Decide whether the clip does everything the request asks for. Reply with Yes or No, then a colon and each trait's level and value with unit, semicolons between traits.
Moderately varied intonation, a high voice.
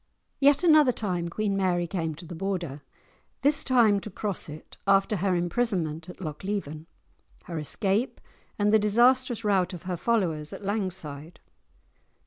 Yes: average, 4.1 semitones; high, 195 Hz